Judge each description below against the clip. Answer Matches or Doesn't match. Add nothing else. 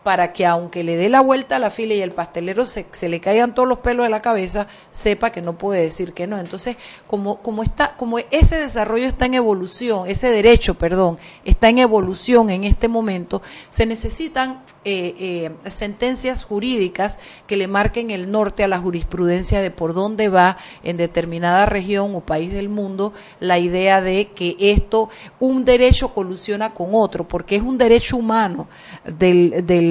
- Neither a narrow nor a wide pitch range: Matches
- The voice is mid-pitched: Doesn't match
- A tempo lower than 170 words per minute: Doesn't match